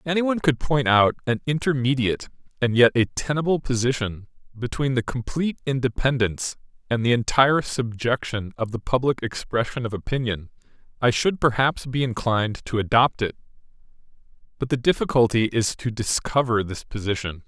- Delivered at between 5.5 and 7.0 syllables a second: Yes, 5.6 syllables/s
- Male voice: Yes, male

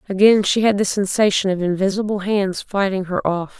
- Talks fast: No, average, 185 wpm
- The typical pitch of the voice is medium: No, high, 195 Hz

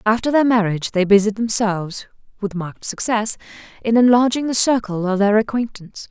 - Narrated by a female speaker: Yes, female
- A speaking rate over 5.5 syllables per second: Yes, 5.7 syllables/s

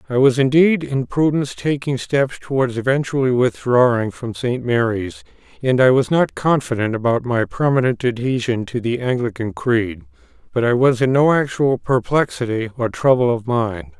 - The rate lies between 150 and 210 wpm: Yes, average, 160 wpm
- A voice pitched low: Yes, low, 125 Hz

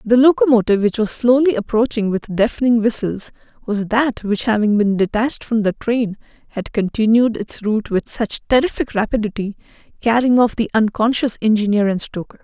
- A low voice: No, high, 225 Hz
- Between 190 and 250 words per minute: No, average, 160 wpm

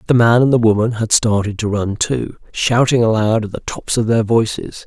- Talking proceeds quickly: Yes, fast, 220 wpm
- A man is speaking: Yes, male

